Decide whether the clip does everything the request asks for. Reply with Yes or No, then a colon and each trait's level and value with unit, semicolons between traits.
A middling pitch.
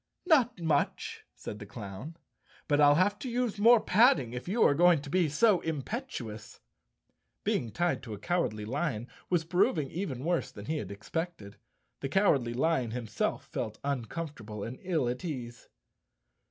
Yes: medium, 150 Hz